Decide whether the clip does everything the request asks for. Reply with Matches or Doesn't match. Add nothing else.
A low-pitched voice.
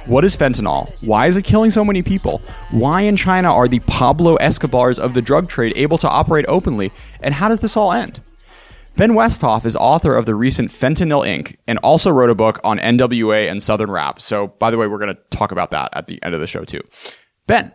Matches